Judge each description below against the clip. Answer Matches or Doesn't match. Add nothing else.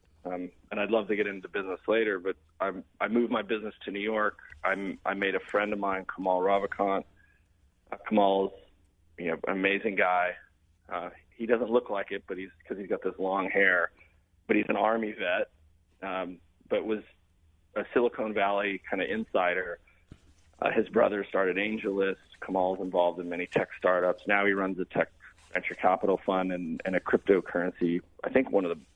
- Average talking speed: Matches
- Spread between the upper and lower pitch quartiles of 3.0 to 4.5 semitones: Doesn't match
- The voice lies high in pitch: Doesn't match